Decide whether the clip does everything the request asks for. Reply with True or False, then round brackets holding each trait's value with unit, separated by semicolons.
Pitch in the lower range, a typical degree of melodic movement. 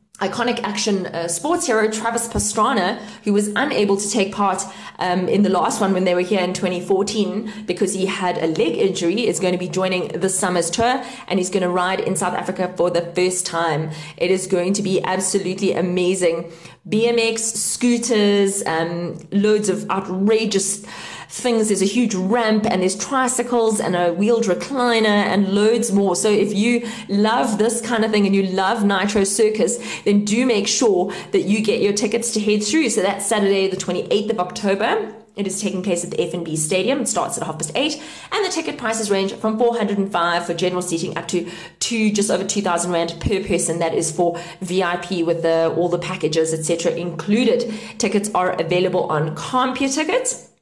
False (195 Hz; 3.4 semitones)